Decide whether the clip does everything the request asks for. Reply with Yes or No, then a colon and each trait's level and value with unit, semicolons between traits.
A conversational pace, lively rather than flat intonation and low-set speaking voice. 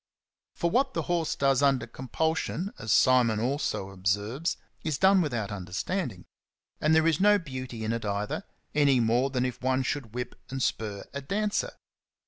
Yes: average, 165 wpm; wide, 6.0 semitones; low, 130 Hz